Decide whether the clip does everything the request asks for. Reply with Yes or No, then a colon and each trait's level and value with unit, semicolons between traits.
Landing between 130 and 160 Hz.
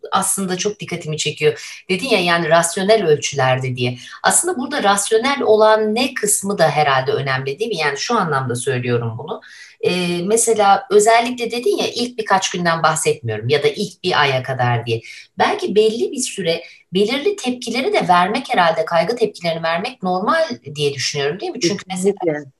No: medium, 185 Hz